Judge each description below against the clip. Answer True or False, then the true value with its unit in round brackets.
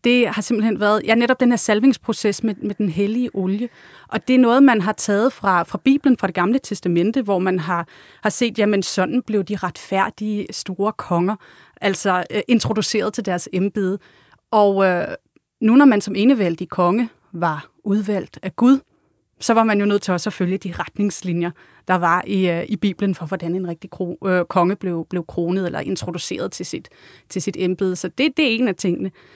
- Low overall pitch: False (200 Hz)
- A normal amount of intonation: True (3.4 semitones)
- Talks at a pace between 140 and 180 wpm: False (200 wpm)